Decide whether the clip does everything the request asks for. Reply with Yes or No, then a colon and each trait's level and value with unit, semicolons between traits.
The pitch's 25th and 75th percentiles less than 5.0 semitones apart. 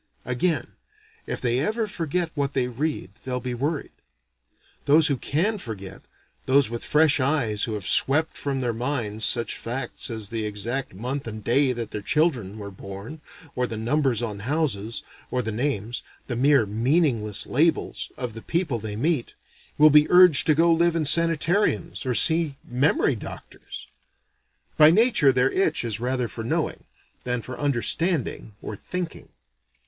No: average, 5.3 semitones